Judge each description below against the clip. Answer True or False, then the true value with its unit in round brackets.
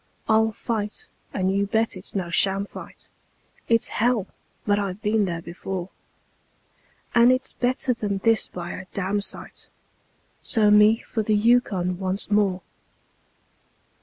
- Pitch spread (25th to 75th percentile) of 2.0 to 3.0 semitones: True (2.7 semitones)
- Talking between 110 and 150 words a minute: True (135 wpm)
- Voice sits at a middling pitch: False (205 Hz)